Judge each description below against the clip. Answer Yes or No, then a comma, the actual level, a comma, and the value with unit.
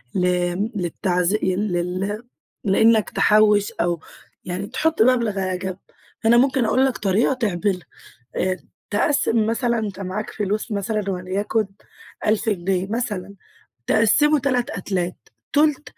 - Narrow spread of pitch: No, average, 3.7 semitones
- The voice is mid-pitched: No, high, 205 Hz